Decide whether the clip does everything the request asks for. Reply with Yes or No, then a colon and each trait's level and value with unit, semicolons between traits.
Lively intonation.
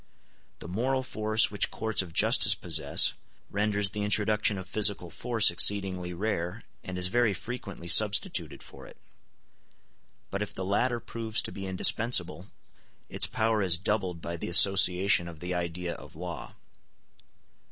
No: average, 3.3 semitones